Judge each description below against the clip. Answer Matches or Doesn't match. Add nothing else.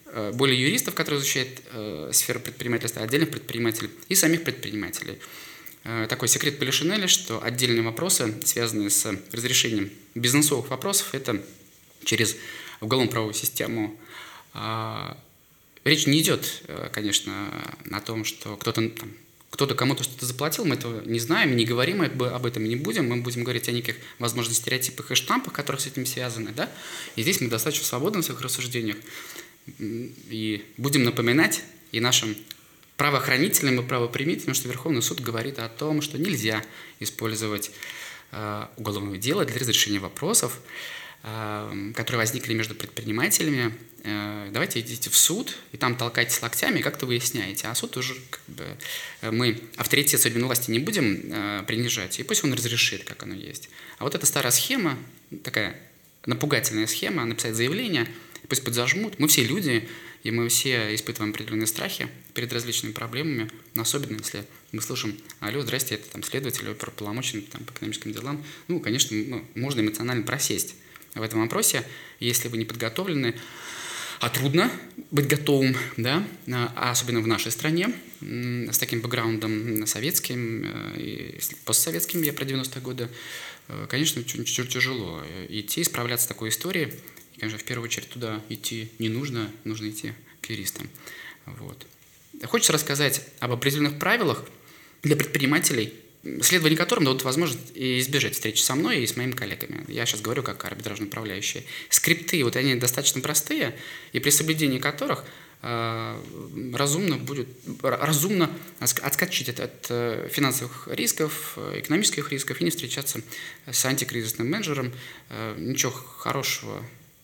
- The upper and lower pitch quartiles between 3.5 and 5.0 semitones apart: Matches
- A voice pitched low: Matches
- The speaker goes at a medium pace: Matches